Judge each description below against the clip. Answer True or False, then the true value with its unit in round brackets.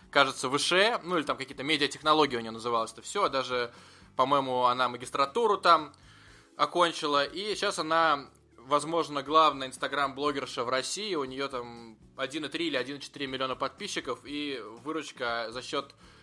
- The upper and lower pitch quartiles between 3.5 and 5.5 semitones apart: True (4.0 semitones)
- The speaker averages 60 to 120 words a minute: False (140 wpm)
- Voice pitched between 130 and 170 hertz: True (140 Hz)